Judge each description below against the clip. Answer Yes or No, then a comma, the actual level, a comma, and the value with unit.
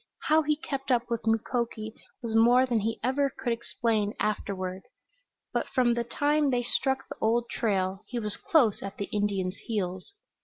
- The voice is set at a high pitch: Yes, high, 230 Hz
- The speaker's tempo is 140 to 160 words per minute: No, average, 175 wpm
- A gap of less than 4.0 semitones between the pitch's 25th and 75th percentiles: Yes, average, 3.6 semitones